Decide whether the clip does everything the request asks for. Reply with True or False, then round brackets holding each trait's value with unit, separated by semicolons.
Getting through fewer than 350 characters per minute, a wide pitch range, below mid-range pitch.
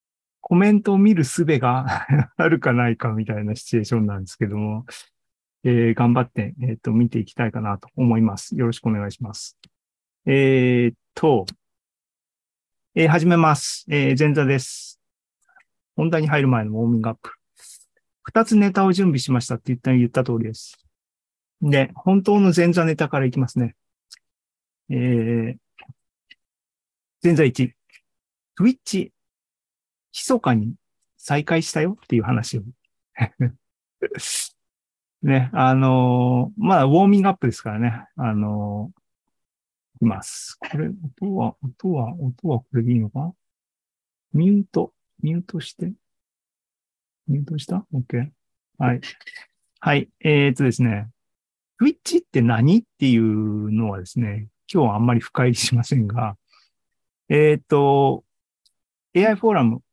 True (275 characters per minute; 5.7 semitones; 130 Hz)